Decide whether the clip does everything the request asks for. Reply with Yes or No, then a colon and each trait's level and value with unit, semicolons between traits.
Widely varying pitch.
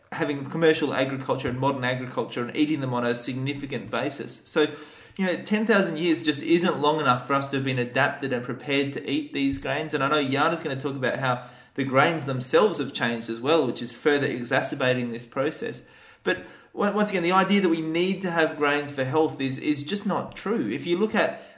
No: average, 3.6 semitones